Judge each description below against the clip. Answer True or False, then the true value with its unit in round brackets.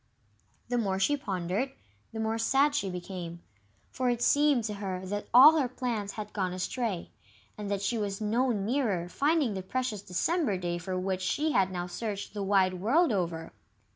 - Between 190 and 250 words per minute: False (180 wpm)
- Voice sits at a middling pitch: False (205 Hz)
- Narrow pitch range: False (5.0 semitones)